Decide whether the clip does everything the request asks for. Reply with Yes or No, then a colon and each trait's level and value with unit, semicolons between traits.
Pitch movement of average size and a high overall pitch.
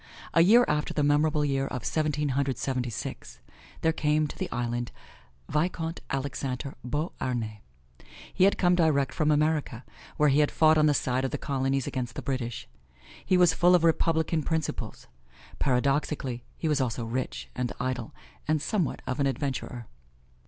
No: average, 3.5 semitones; medium, 140 Hz